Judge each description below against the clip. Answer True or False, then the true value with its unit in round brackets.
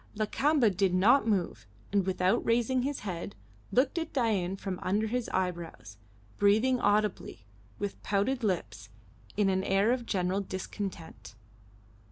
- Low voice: False (200 Hz)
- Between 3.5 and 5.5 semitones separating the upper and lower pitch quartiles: True (4.1 semitones)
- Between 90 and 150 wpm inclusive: True (135 wpm)